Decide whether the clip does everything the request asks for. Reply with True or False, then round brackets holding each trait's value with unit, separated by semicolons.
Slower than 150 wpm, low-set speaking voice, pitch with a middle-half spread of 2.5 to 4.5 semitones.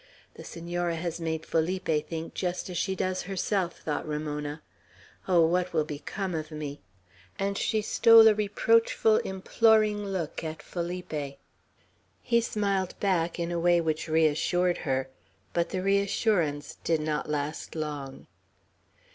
False (140 wpm; 170 Hz; 3.7 semitones)